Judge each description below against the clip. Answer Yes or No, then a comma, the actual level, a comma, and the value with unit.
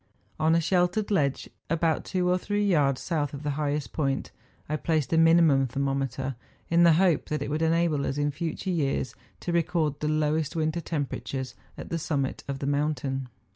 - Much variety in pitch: No, average, 3.2 semitones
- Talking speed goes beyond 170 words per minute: Yes, average, 185 wpm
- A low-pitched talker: No, medium, 155 Hz